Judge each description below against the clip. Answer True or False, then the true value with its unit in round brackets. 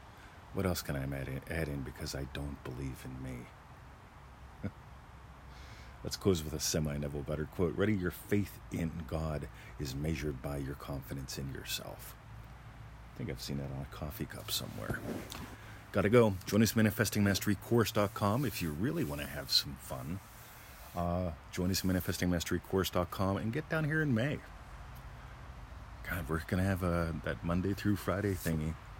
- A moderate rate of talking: True (165 wpm)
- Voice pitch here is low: True (90 Hz)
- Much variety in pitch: True (5.8 semitones)